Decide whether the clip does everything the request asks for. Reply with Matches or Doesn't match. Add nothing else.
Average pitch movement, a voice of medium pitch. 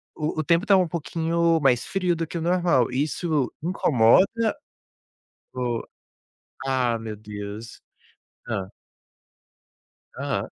Doesn't match